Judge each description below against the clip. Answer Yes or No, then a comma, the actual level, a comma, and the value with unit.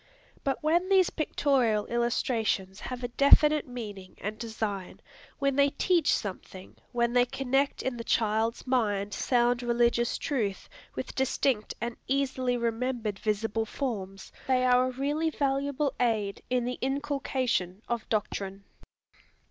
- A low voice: No, high, 245 Hz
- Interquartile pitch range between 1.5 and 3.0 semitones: No, average, 3.8 semitones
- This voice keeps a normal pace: No, slow, 130 wpm